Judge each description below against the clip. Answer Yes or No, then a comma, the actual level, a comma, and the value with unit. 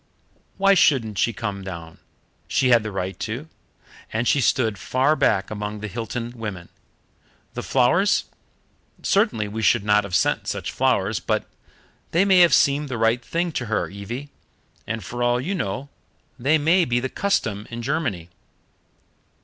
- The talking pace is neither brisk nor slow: Yes, average, 160 wpm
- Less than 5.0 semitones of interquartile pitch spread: No, wide, 5.5 semitones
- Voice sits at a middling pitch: No, low, 120 Hz